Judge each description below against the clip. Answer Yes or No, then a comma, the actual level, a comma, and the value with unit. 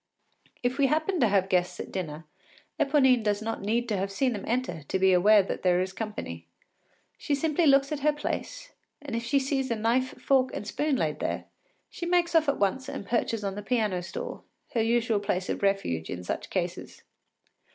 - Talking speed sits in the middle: No, fast, 210 wpm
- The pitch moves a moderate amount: No, wide, 6.0 semitones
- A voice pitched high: Yes, high, 230 Hz